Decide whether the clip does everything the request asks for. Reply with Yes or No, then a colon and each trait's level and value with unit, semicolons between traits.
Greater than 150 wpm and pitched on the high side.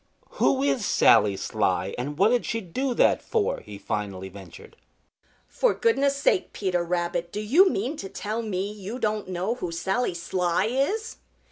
Yes: average, 165 wpm; high, 200 Hz